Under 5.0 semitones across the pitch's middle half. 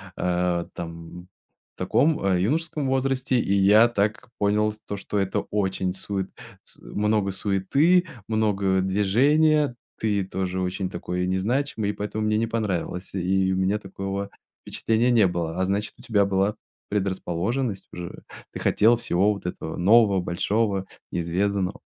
Yes: average, 2.9 semitones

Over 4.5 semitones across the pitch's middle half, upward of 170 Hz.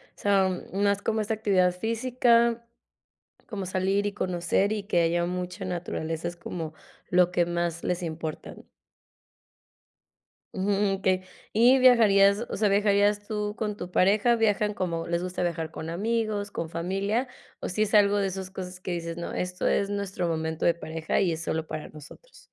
No: average, 3.2 semitones; high, 190 Hz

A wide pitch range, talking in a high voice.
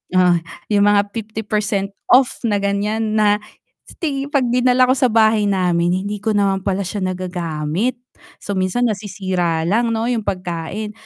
No: average, 3.2 semitones; high, 205 Hz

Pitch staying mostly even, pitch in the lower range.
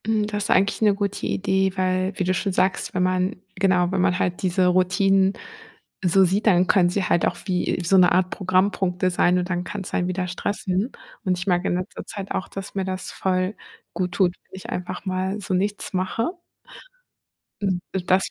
No: narrow, 1.3 semitones; medium, 185 Hz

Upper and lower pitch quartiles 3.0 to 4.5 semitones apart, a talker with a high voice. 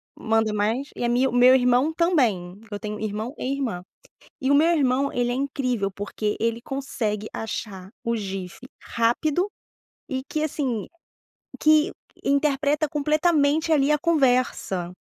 No: average, 5.0 semitones; very high, 255 Hz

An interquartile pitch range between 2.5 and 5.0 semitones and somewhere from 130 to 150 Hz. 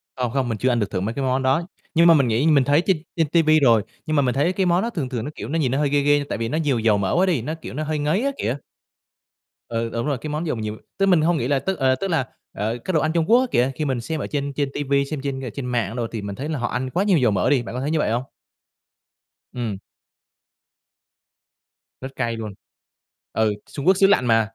Yes: average, 4.7 semitones; medium, 140 Hz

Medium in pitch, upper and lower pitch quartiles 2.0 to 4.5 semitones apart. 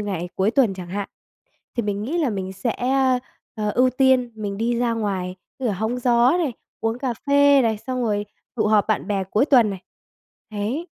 No: high, 225 Hz; average, 3.9 semitones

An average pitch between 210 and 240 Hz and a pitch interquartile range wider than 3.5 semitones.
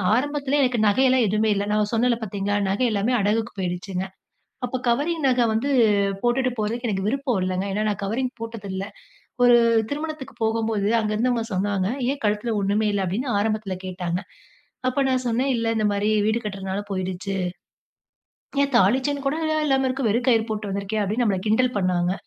Yes: high, 220 Hz; average, 4.1 semitones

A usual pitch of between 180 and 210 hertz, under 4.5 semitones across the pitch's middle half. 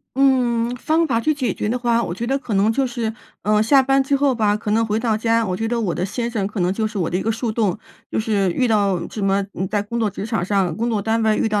No: high, 225 Hz; average, 2.8 semitones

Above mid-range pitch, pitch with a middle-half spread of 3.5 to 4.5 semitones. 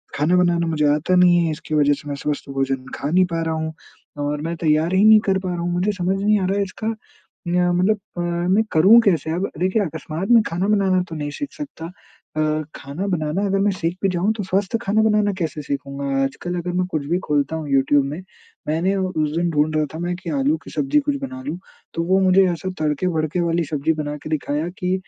No: medium, 175 Hz; average, 3.8 semitones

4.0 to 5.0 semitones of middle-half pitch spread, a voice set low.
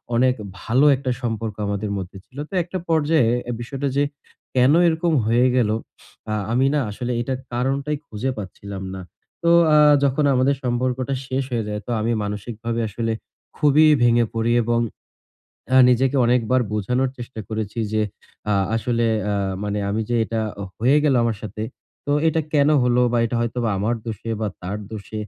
No: average, 3.3 semitones; low, 120 Hz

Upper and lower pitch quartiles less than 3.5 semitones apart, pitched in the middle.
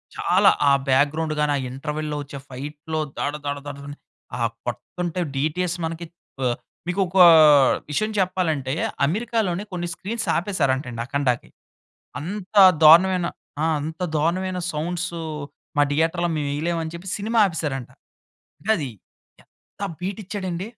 No: average, 4.1 semitones; medium, 165 Hz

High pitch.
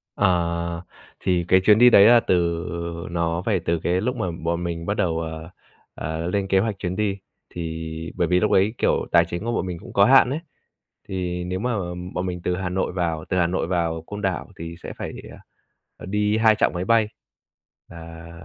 No: very low, 90 Hz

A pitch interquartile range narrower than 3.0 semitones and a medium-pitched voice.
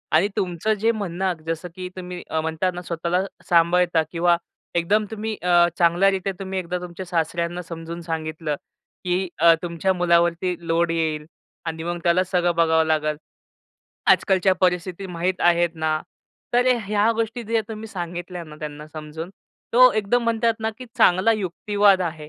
Yes: narrow, 2.4 semitones; medium, 175 Hz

